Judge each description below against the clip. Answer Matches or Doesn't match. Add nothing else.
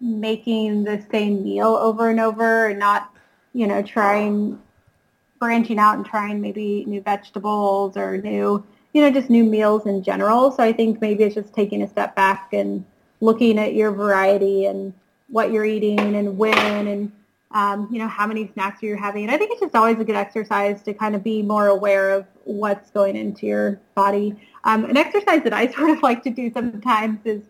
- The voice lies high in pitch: Matches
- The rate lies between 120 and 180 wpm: Doesn't match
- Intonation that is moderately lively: Doesn't match